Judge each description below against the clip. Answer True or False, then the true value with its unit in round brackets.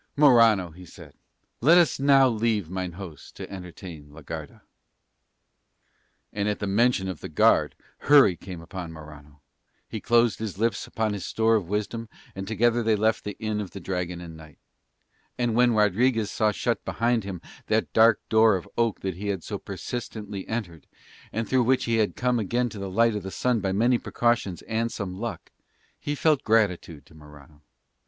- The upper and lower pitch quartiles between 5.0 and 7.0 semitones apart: False (4.2 semitones)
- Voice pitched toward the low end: True (105 Hz)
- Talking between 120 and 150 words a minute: False (185 wpm)